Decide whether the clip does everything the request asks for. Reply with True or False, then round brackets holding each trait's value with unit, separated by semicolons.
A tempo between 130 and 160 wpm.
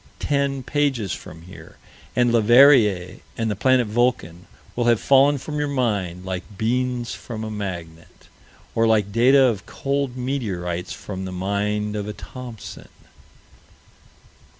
True (135 wpm)